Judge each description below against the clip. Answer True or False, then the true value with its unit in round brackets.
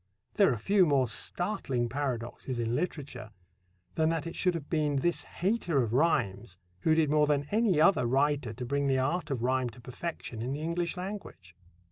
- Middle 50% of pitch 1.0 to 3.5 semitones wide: False (5.3 semitones)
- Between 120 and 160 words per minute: False (185 wpm)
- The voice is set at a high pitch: False (145 Hz)